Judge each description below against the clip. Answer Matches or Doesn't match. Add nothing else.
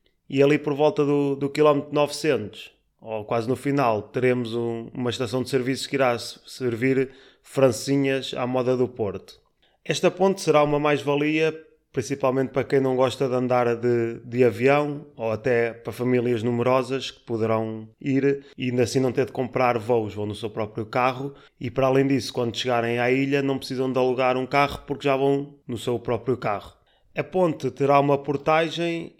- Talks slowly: Doesn't match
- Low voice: Matches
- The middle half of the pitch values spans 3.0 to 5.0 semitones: Doesn't match